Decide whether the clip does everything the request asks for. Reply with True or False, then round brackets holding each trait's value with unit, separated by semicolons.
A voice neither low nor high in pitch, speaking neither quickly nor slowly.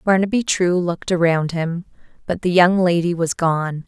True (175 Hz; 170 wpm)